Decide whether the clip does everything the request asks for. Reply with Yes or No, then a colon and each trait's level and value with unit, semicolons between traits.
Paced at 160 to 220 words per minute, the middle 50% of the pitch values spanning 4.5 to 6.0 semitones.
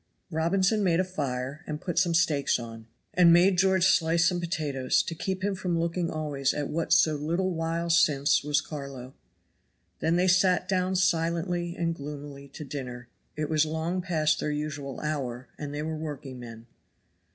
No: average, 170 wpm; average, 3.5 semitones